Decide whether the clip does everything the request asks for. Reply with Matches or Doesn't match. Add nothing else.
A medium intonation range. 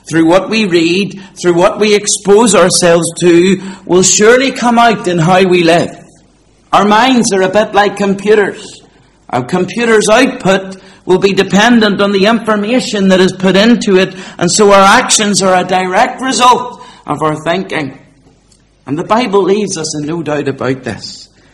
Matches